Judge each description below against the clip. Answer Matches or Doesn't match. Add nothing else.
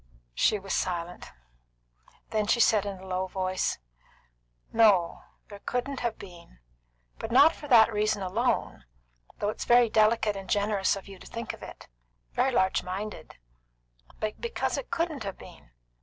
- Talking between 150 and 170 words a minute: Matches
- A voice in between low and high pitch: Doesn't match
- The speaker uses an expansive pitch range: Doesn't match